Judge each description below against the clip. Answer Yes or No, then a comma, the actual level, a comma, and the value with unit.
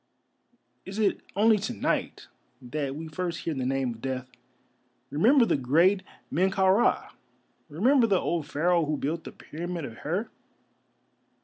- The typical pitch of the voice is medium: Yes, medium, 170 Hz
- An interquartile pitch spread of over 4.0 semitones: Yes, average, 5.1 semitones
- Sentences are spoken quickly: No, average, 150 wpm